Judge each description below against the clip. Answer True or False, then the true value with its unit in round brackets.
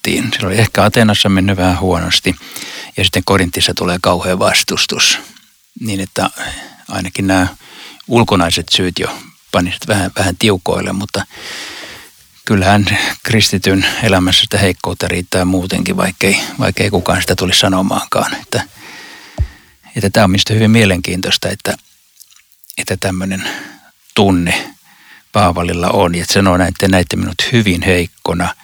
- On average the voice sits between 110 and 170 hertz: False (95 Hz)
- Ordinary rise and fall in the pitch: False (2.2 semitones)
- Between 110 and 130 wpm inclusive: True (125 wpm)